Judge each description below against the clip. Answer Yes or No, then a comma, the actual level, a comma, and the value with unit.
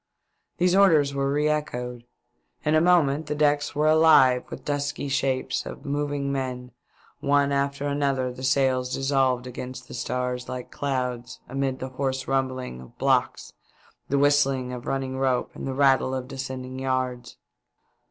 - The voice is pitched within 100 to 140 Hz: Yes, low, 135 Hz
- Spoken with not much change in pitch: Yes, narrow, 1.9 semitones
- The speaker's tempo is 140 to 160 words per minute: Yes, average, 150 wpm